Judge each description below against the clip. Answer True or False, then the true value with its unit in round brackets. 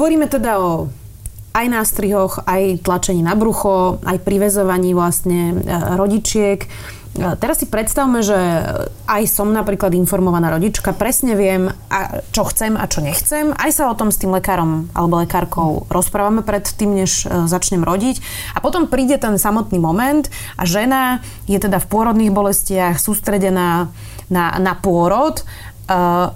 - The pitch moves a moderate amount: True (3.6 semitones)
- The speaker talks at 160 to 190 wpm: False (140 wpm)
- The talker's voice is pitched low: False (195 Hz)